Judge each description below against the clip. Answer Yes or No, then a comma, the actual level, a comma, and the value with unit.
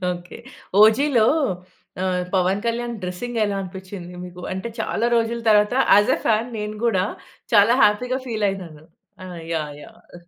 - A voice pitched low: No, high, 210 Hz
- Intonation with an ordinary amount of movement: Yes, average, 4.1 semitones